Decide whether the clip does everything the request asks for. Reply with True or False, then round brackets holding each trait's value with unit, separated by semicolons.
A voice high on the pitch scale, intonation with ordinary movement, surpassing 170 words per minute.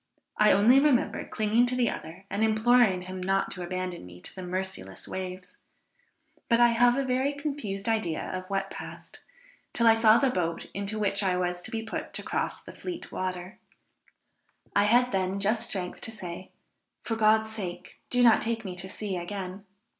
True (200 Hz; 4.0 semitones; 185 wpm)